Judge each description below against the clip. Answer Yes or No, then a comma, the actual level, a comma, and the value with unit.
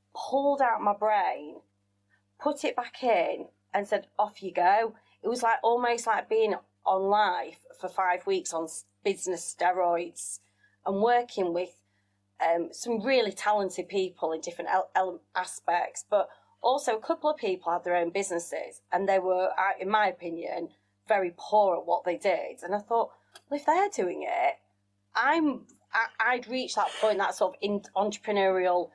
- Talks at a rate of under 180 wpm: Yes, average, 170 wpm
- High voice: Yes, high, 195 Hz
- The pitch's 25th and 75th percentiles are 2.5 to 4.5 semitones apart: No, average, 5.0 semitones